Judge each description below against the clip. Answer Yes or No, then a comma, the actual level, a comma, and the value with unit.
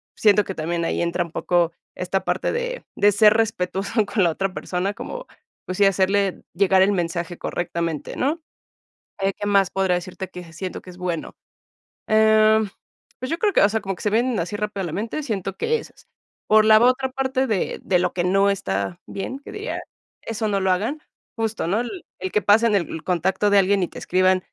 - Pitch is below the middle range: No, high, 195 Hz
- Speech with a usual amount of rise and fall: Yes, average, 3.2 semitones